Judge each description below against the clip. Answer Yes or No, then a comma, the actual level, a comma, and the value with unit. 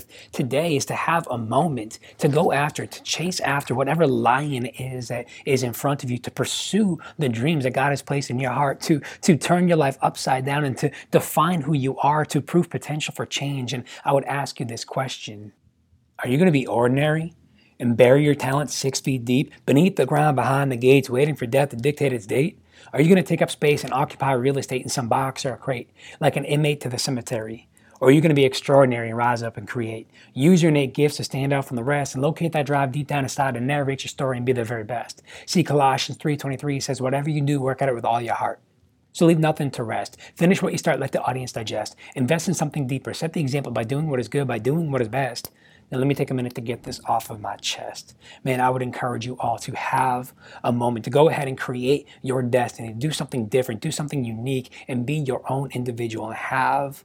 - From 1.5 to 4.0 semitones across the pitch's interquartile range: Yes, average, 2.8 semitones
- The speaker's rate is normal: No, fast, 240 wpm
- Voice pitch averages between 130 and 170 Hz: Yes, low, 135 Hz